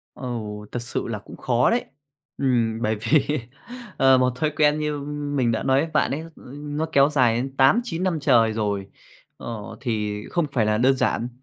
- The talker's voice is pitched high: No, low, 130 Hz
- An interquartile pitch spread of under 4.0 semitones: No, average, 4.5 semitones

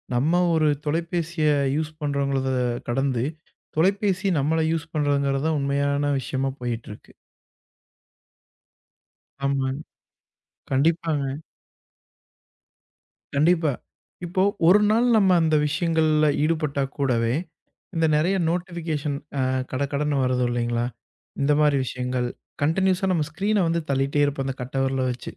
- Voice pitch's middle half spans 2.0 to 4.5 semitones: Yes, average, 3.4 semitones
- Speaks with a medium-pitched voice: Yes, medium, 150 Hz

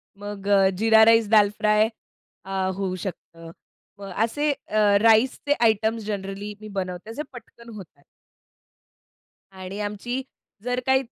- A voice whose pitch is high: Yes, high, 210 Hz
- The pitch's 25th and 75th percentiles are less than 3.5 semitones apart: Yes, narrow, 2.6 semitones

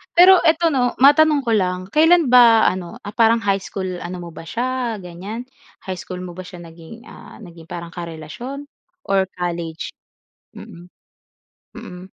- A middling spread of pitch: No, wide, 6.0 semitones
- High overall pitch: Yes, high, 195 Hz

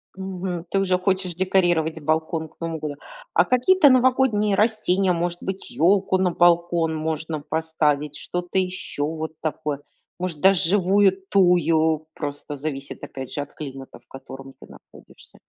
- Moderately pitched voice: Yes, medium, 170 Hz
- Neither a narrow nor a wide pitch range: Yes, average, 3.4 semitones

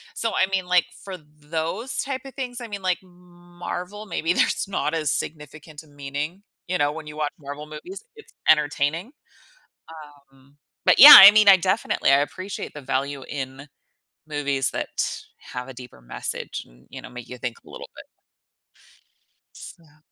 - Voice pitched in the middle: Yes, medium, 155 Hz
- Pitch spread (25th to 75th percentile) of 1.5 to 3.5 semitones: No, average, 4.7 semitones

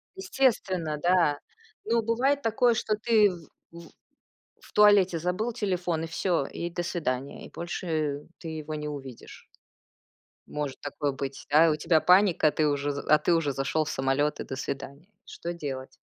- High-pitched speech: No, medium, 165 Hz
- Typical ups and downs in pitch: Yes, average, 4.5 semitones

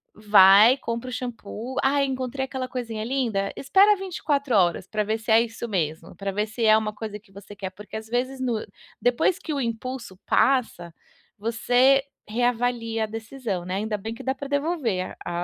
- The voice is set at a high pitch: Yes, high, 230 Hz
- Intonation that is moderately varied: Yes, average, 3.8 semitones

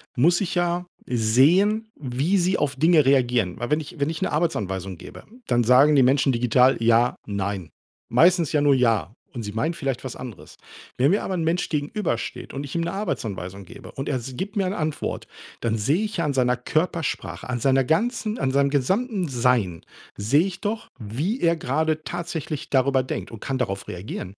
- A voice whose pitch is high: No, medium, 140 Hz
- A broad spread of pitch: Yes, wide, 5.9 semitones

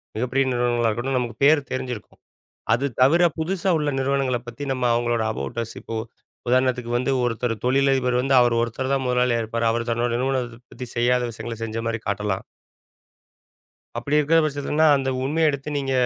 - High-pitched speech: No, low, 125 Hz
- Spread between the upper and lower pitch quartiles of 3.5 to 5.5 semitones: No, narrow, 2.5 semitones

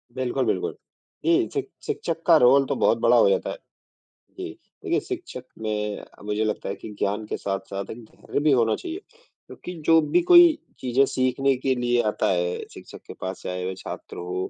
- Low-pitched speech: Yes, low, 125 Hz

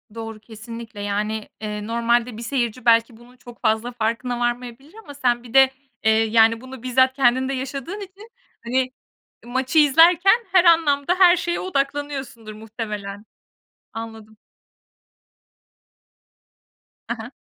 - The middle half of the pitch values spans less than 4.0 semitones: Yes, average, 3.6 semitones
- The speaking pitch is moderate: No, high, 240 Hz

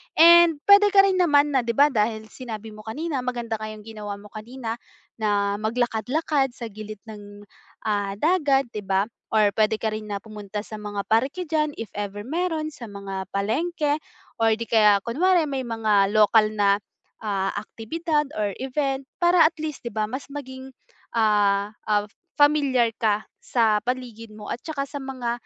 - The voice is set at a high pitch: Yes, high, 230 Hz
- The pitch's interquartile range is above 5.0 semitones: Yes, wide, 5.4 semitones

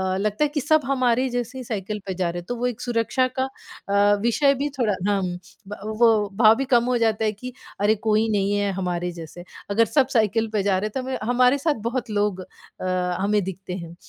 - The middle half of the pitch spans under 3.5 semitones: No, average, 3.9 semitones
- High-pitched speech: Yes, high, 215 Hz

